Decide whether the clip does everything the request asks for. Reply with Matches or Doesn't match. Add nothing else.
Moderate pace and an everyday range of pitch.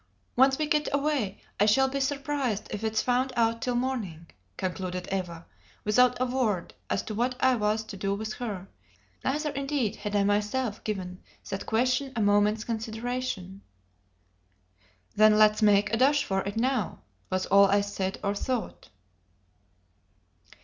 Matches